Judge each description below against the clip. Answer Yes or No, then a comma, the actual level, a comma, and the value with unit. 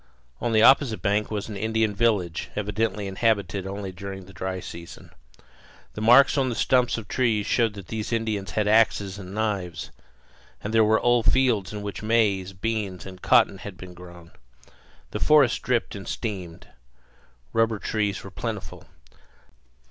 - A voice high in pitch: No, low, 105 Hz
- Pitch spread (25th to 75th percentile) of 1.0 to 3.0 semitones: Yes, average, 2.7 semitones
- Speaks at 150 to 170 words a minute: Yes, average, 160 wpm